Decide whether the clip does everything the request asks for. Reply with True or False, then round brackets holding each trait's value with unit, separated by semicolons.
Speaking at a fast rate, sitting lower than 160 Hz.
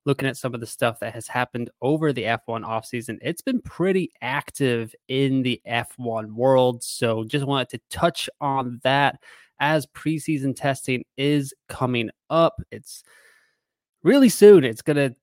False (160 wpm; 135 Hz)